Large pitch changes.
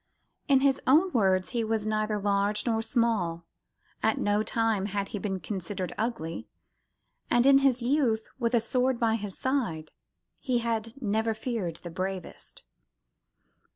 No: average, 3.3 semitones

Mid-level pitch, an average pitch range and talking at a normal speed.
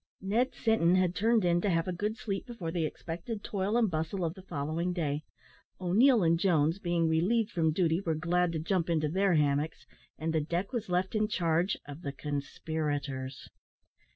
Yes: medium, 175 Hz; average, 3.6 semitones; average, 185 wpm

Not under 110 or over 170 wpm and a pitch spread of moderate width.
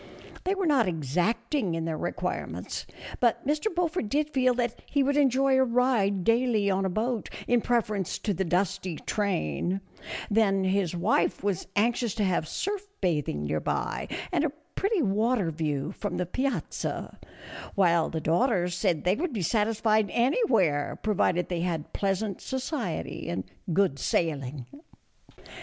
No: average, 150 wpm; wide, 6.1 semitones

